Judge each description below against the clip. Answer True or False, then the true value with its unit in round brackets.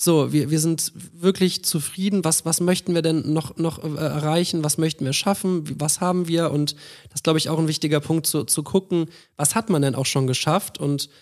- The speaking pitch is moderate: True (160 Hz)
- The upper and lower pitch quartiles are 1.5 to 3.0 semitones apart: True (2.6 semitones)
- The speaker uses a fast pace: True (220 wpm)